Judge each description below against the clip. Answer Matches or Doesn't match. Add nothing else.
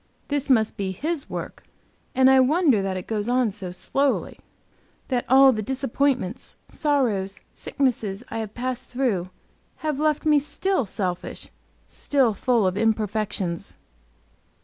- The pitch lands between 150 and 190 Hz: Doesn't match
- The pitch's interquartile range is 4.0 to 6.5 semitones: Matches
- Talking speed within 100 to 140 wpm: Matches